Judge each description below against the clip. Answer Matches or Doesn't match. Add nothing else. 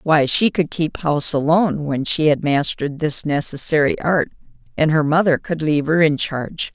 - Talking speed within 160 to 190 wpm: Matches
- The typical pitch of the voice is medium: Matches